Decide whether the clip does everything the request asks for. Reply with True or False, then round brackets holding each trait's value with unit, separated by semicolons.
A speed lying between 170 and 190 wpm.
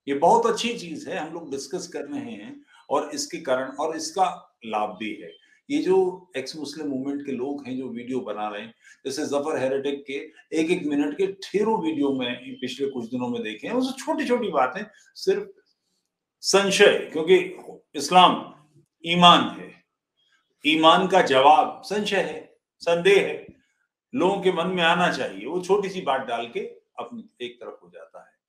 True (175 wpm)